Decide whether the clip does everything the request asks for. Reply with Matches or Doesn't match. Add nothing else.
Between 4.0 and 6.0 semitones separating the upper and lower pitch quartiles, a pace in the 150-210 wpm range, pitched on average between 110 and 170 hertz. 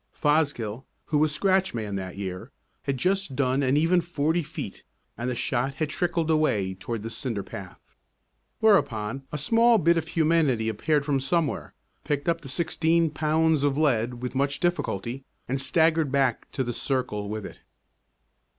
Matches